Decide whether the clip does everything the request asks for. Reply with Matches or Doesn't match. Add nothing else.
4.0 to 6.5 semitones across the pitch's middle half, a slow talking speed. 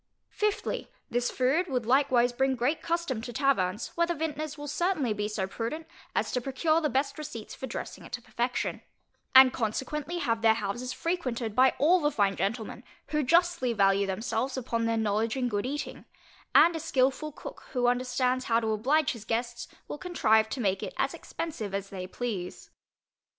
Doesn't match